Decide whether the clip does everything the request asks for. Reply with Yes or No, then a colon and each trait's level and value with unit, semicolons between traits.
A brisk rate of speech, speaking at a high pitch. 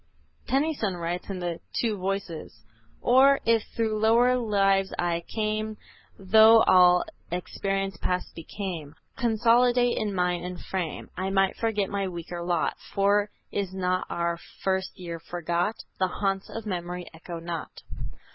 No: slow, 135 wpm; high, 195 Hz